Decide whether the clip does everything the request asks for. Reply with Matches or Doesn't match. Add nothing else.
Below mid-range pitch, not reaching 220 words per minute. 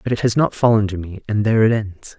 Doesn't match